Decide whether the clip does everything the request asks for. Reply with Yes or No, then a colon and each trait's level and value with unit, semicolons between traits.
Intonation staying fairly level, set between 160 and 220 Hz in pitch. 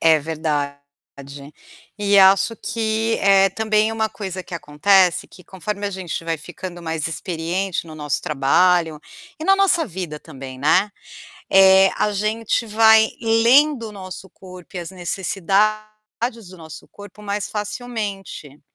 No: average, 4.2 semitones; high, 190 Hz